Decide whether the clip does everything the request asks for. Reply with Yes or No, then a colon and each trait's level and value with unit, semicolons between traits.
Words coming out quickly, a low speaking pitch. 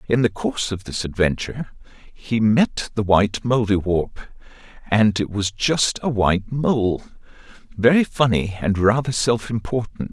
No: average, 140 wpm; low, 110 Hz